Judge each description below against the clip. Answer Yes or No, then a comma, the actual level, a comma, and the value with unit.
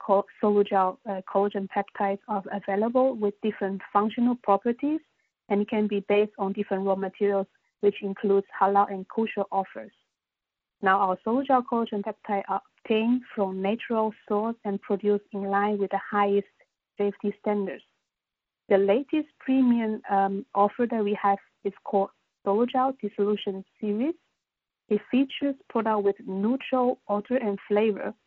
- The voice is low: No, high, 205 Hz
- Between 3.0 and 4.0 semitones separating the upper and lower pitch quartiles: No, narrow, 2.4 semitones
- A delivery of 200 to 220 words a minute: No, average, 140 wpm